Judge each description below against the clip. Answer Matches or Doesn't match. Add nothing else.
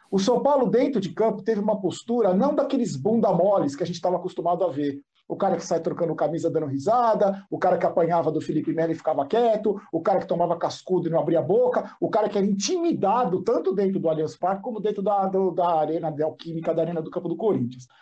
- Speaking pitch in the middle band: Matches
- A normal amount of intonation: Matches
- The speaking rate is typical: Doesn't match